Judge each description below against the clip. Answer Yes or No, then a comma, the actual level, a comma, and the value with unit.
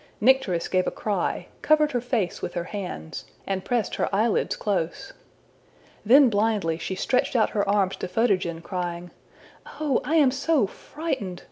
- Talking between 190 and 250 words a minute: No, average, 155 wpm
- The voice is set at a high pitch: Yes, high, 205 Hz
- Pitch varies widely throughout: Yes, wide, 5.7 semitones